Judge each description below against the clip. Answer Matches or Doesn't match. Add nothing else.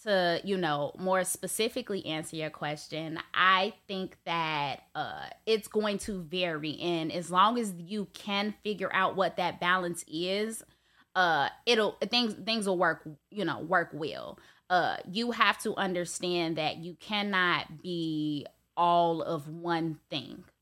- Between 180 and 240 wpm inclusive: Doesn't match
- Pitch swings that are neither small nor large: Matches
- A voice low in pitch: Doesn't match